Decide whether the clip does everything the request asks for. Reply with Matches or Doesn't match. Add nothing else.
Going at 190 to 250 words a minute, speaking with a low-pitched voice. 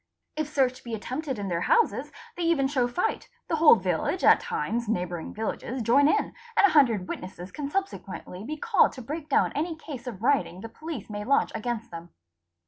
Doesn't match